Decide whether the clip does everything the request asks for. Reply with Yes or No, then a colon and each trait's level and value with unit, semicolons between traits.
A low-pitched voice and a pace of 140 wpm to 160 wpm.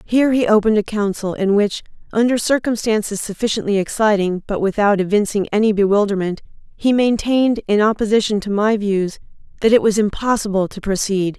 No: high, 210 Hz; average, 155 wpm